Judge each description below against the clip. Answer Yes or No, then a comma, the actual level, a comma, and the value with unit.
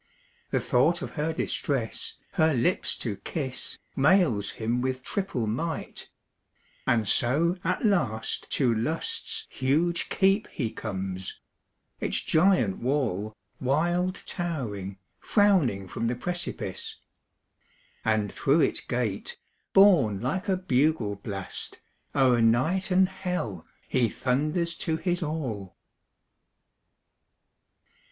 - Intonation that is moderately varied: No, wide, 7.6 semitones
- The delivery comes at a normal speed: No, slow, 110 wpm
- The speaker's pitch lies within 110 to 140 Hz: Yes, low, 135 Hz